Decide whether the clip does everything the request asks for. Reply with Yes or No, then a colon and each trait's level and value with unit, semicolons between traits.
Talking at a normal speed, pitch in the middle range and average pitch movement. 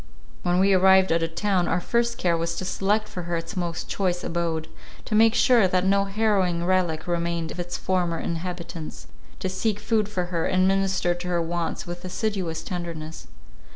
No: average, 190 wpm; medium, 180 Hz; narrow, 2.3 semitones